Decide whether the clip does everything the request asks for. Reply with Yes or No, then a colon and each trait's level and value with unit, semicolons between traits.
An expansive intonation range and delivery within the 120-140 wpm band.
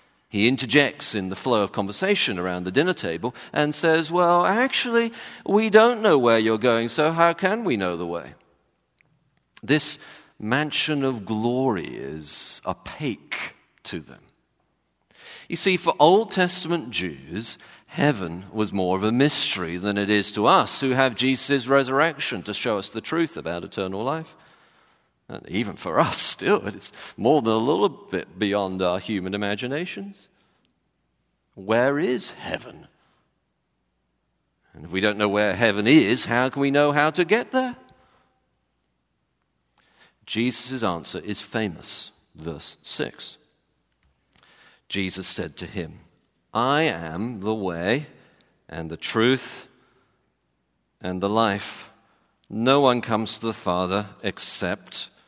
Yes: wide, 7.7 semitones; slow, 135 wpm